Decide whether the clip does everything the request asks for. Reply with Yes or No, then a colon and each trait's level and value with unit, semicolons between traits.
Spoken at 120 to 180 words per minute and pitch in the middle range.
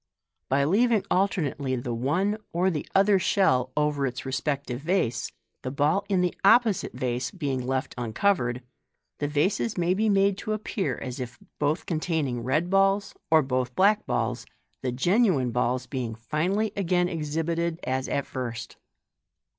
Yes: average, 150 wpm; medium, 150 Hz